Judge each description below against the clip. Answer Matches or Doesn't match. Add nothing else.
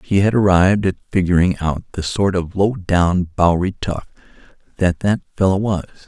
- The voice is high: Doesn't match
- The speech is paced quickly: Doesn't match